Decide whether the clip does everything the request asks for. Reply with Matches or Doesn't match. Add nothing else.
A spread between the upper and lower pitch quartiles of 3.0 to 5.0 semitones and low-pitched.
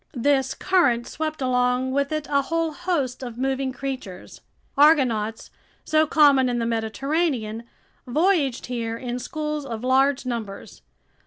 Doesn't match